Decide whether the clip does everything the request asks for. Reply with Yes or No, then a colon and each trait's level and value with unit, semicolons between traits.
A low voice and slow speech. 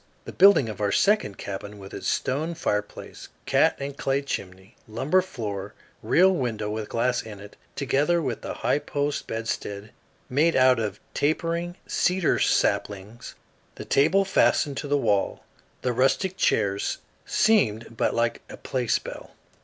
No: low, 125 Hz; average, 150 wpm